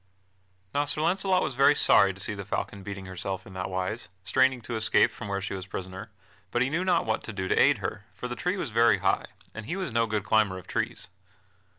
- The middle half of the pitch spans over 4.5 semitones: Yes, wide, 5.6 semitones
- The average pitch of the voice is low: Yes, low, 110 Hz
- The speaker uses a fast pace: Yes, fast, 240 wpm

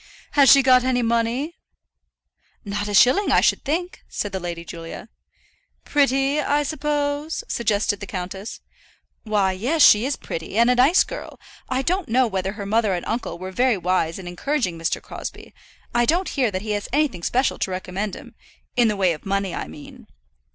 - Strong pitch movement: Yes, wide, 6.2 semitones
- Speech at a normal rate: Yes, average, 185 wpm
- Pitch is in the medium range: No, high, 225 Hz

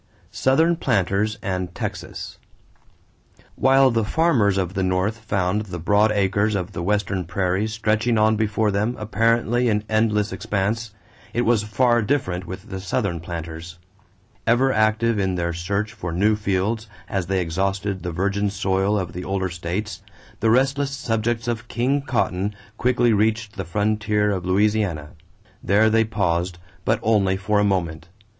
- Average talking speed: Yes, average, 150 wpm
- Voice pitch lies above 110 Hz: No, low, 105 Hz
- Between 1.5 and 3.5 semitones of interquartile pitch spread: Yes, average, 3.0 semitones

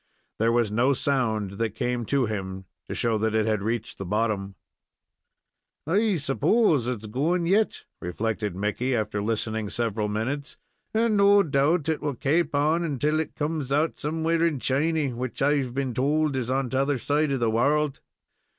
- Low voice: Yes, low, 130 Hz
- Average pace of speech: Yes, average, 170 wpm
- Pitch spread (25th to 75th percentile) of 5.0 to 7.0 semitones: Yes, wide, 5.4 semitones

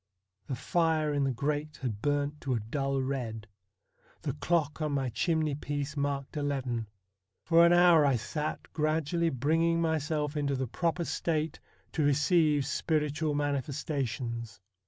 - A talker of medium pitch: Yes, medium, 145 Hz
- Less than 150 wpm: Yes, average, 140 wpm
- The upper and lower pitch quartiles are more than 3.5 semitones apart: No, average, 2.7 semitones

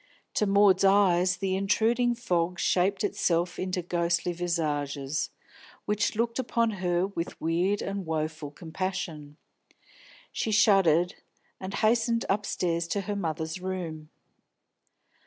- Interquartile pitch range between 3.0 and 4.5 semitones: Yes, average, 3.3 semitones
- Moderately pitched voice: Yes, medium, 180 Hz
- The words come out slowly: Yes, slow, 115 wpm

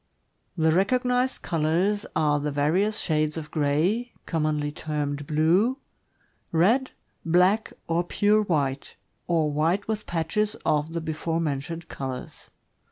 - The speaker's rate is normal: No, slow, 125 wpm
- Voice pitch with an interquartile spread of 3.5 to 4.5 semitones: No, average, 4.9 semitones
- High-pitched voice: No, medium, 165 Hz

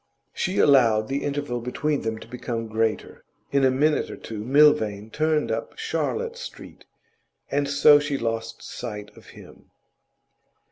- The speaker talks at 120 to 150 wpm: Yes, average, 145 wpm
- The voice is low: Yes, low, 130 Hz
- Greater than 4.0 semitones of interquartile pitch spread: Yes, average, 4.6 semitones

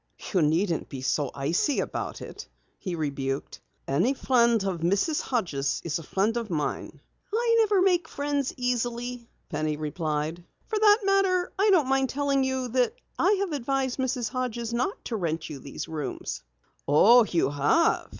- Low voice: No, high, 235 Hz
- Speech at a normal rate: Yes, average, 160 wpm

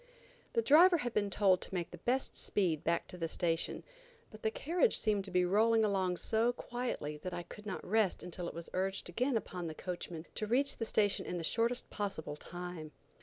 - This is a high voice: Yes, high, 195 Hz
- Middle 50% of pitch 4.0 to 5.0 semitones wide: Yes, average, 4.4 semitones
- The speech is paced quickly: Yes, fast, 210 wpm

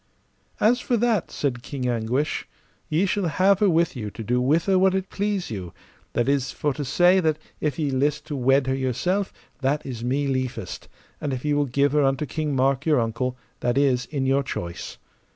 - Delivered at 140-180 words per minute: No, fast, 205 wpm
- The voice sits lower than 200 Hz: Yes, medium, 140 Hz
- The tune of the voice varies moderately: Yes, average, 4.1 semitones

